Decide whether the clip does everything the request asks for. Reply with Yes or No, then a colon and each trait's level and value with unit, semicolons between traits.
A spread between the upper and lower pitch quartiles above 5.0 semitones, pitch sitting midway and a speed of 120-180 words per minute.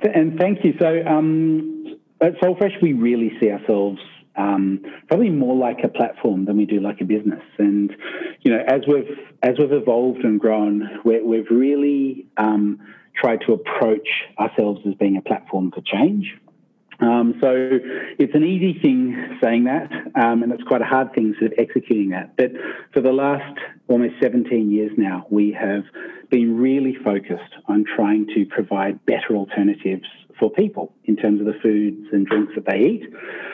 No: wide, 5.5 semitones; low, 115 Hz; average, 170 wpm